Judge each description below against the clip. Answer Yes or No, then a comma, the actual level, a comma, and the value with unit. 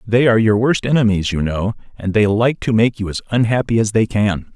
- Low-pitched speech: Yes, low, 110 Hz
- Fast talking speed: Yes, fast, 235 wpm